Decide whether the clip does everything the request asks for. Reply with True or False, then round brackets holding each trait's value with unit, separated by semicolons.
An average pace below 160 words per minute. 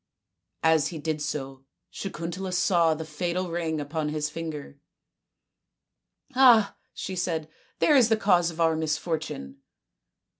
True (140 wpm)